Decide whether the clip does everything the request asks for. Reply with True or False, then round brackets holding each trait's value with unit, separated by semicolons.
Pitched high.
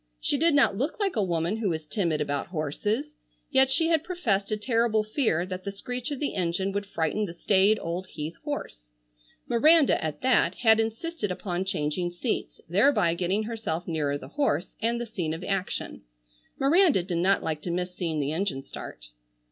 True (195 Hz)